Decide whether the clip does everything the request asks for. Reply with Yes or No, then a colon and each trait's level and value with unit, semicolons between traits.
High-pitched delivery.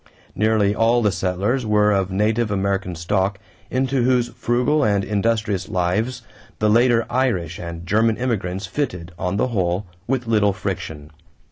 No: low, 105 Hz